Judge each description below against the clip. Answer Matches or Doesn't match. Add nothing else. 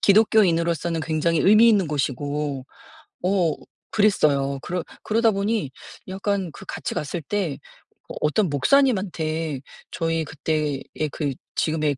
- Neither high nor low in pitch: Matches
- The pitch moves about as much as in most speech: Matches